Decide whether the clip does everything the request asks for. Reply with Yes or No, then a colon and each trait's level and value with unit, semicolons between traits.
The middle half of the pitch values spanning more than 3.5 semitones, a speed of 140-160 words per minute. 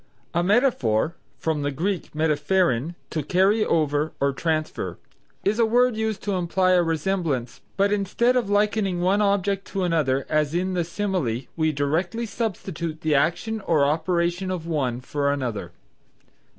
Yes: average, 4.7 semitones; average, 150 wpm